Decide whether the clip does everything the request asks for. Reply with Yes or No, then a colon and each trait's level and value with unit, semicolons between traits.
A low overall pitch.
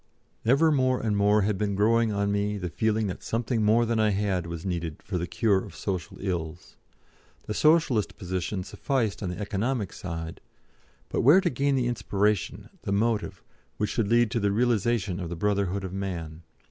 Yes: low, 105 Hz